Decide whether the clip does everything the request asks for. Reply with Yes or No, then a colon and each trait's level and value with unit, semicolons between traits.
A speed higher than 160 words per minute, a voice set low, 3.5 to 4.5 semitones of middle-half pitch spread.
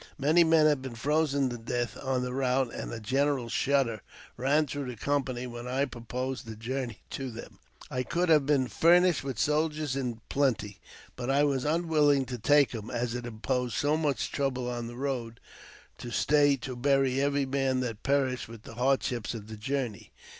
No: average, 190 wpm; low, 130 Hz; average, 2.8 semitones